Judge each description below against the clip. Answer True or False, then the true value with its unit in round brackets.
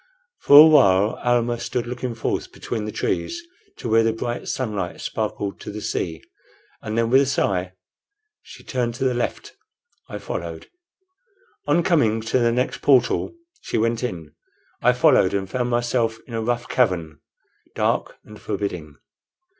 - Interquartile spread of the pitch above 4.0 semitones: False (3.0 semitones)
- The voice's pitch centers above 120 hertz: False (115 Hz)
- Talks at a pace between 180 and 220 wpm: False (160 wpm)